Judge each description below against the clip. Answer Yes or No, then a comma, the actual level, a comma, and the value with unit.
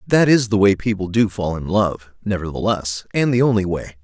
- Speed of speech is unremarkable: No, fast, 210 wpm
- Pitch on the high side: No, low, 100 Hz